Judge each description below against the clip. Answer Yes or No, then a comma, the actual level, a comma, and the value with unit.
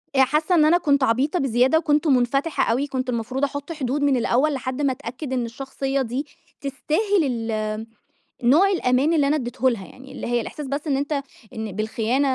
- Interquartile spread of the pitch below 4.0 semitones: Yes, average, 3.3 semitones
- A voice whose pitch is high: Yes, very high, 270 Hz